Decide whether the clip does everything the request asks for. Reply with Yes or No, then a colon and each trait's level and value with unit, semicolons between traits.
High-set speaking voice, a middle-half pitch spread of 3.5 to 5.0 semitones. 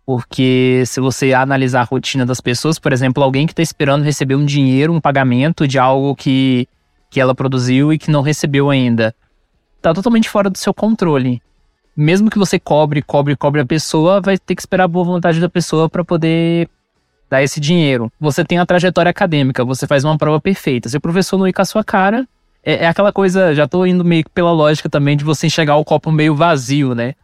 No: medium, 150 Hz; average, 4.6 semitones